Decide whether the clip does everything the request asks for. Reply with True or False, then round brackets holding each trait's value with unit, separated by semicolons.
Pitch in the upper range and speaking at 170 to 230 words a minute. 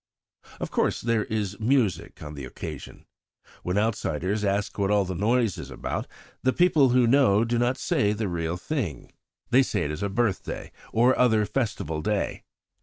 False (105 Hz; 175 wpm)